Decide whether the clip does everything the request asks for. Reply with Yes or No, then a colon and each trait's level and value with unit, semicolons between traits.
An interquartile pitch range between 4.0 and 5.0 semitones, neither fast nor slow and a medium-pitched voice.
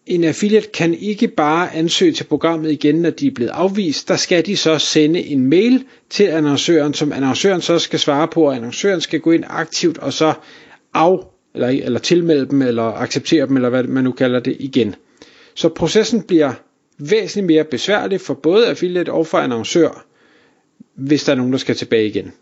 Yes: average, 4.5 semitones; average, 195 wpm; medium, 155 Hz